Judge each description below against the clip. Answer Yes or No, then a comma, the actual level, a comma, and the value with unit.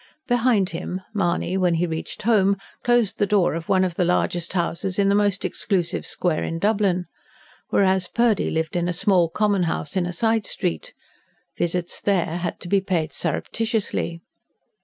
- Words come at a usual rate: Yes, average, 170 wpm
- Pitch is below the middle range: No, medium, 185 Hz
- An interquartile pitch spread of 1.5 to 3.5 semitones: Yes, average, 2.9 semitones